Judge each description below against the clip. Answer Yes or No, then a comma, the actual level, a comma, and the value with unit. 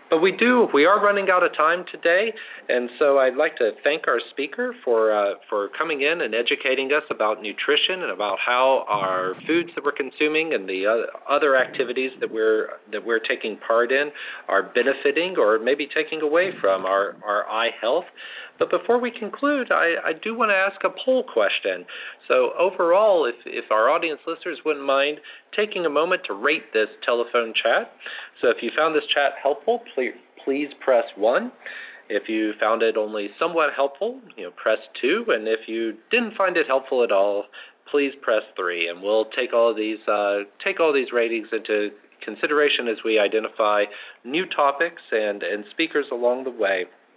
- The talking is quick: No, average, 185 wpm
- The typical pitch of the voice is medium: Yes, medium, 145 Hz